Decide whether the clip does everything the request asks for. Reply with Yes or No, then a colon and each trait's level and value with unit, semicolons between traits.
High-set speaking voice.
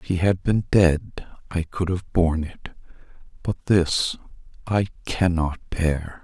No: very low, 90 Hz